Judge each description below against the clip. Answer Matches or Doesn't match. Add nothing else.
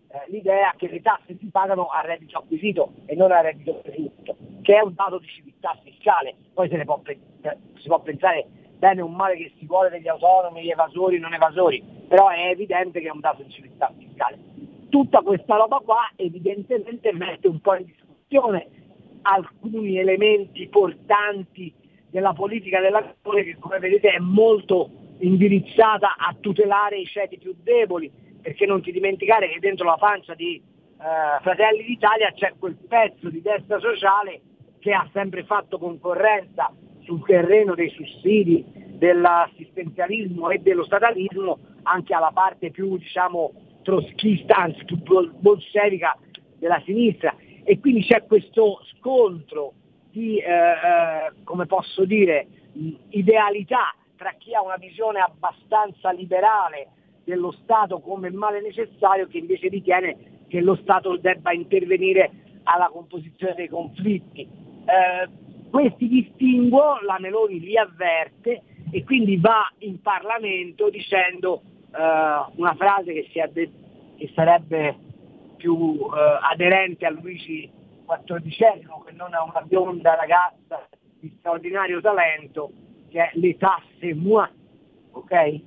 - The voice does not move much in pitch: Doesn't match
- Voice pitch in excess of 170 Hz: Matches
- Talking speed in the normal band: Matches